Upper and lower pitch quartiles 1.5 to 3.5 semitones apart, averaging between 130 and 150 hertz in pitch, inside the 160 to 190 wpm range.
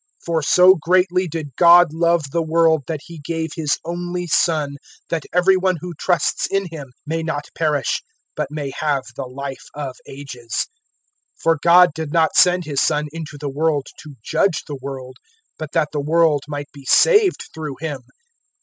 No: average, 2.9 semitones; medium, 160 Hz; average, 180 wpm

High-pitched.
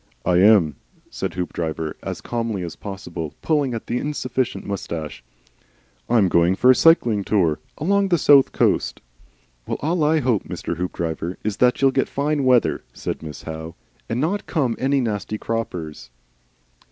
No: low, 110 Hz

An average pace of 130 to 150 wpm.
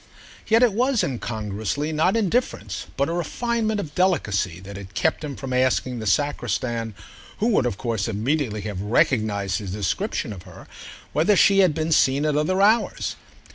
No: average, 170 wpm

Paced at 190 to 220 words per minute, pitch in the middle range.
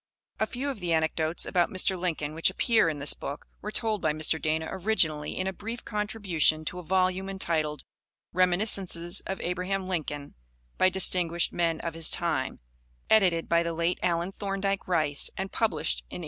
No: average, 175 wpm; medium, 175 Hz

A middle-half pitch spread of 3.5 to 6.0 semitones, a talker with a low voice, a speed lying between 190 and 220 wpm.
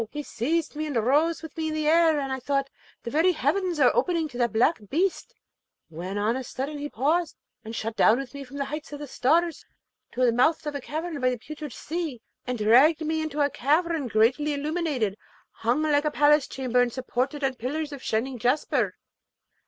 No: average, 3.8 semitones; very high, 285 Hz; fast, 205 wpm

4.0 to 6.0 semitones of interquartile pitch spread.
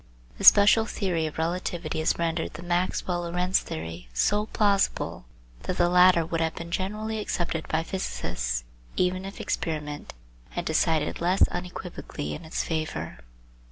No: narrow, 2.6 semitones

